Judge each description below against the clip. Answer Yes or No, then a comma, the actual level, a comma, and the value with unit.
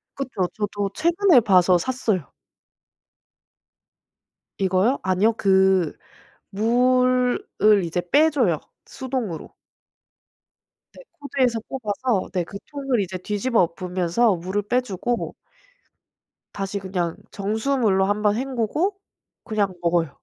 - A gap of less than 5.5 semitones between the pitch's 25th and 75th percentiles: Yes, average, 5.1 semitones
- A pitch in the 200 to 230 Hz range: Yes, high, 210 Hz